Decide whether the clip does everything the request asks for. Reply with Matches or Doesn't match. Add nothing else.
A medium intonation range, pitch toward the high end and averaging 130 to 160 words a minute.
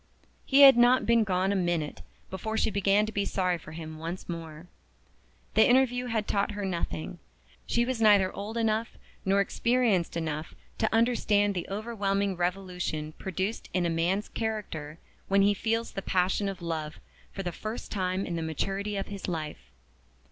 Doesn't match